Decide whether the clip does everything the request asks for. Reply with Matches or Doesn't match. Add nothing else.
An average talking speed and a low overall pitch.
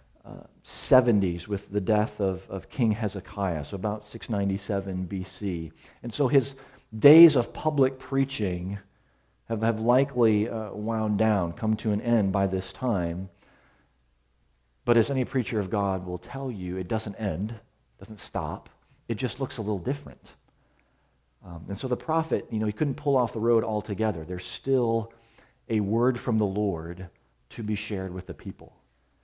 Matches